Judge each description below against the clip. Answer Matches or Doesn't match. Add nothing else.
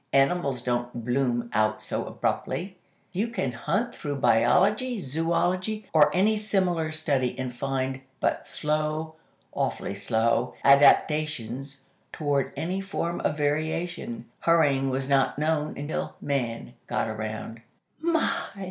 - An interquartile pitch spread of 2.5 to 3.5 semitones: Doesn't match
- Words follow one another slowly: Matches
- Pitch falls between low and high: Matches